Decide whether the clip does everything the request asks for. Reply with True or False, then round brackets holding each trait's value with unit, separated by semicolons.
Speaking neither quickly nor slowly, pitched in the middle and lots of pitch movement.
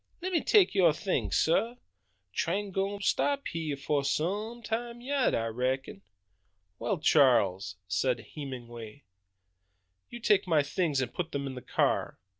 True (145 wpm; 160 Hz; 8.2 semitones)